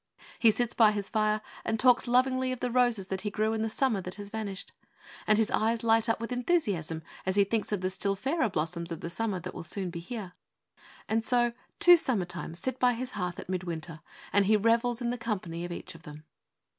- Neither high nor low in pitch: No, high, 215 Hz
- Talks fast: Yes, fast, 230 wpm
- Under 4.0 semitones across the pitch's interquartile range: No, average, 4.5 semitones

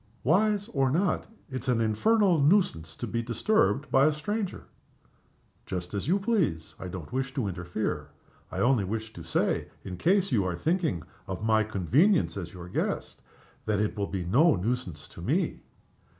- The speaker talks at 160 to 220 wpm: Yes, average, 170 wpm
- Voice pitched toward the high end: No, low, 115 Hz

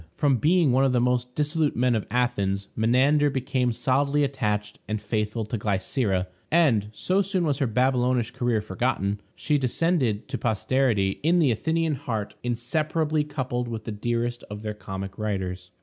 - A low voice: Yes, low, 125 Hz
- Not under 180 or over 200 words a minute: No, average, 165 wpm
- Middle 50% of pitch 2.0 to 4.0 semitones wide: No, average, 4.8 semitones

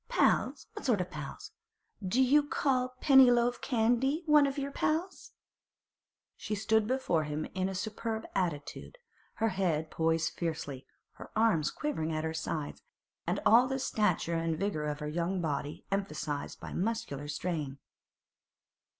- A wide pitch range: Yes, wide, 7.8 semitones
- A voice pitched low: No, high, 190 Hz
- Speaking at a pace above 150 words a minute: No, average, 140 wpm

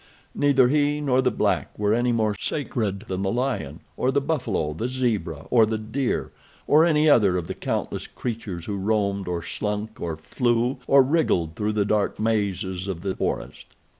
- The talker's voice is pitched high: No, low, 110 Hz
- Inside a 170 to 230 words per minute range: Yes, average, 180 wpm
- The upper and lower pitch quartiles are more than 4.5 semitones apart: Yes, average, 4.9 semitones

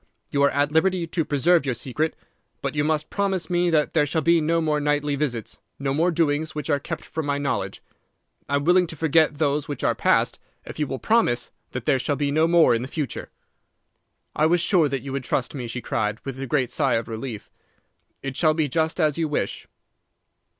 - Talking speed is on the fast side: Yes, fast, 220 wpm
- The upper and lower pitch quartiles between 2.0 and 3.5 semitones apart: Yes, average, 2.9 semitones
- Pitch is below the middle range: No, medium, 150 Hz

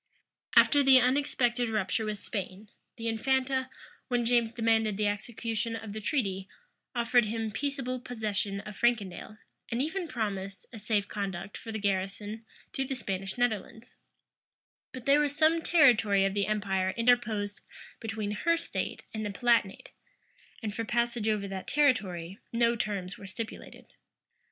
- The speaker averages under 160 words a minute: Yes, average, 150 wpm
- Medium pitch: No, high, 220 Hz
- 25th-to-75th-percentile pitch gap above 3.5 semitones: No, average, 3.2 semitones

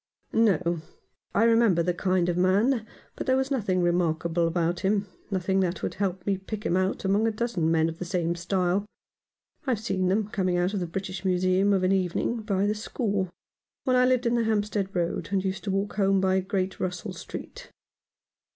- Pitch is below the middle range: No, high, 190 Hz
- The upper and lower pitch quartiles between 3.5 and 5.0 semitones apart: No, average, 2.8 semitones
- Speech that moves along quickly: Yes, fast, 210 wpm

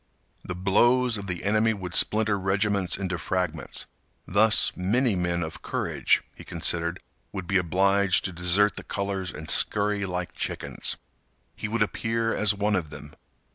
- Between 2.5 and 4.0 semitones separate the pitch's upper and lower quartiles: Yes, average, 2.8 semitones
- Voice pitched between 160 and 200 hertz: No, very low, 95 Hz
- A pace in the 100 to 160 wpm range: Yes, average, 155 wpm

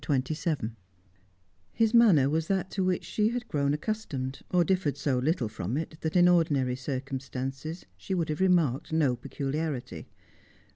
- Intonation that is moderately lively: Yes, average, 5.0 semitones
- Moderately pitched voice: Yes, medium, 155 Hz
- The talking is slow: No, average, 155 wpm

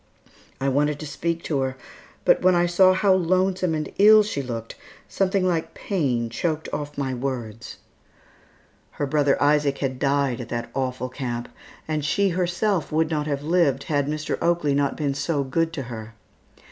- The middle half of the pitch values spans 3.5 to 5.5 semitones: Yes, average, 4.2 semitones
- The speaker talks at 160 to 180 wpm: Yes, average, 170 wpm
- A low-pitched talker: No, medium, 145 Hz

